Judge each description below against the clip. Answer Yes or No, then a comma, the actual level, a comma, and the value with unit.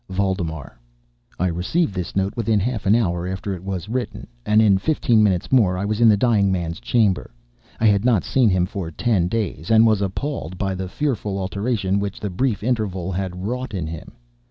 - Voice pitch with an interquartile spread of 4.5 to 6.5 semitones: No, average, 3.4 semitones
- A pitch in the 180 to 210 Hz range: No, low, 100 Hz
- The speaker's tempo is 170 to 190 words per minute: No, average, 200 wpm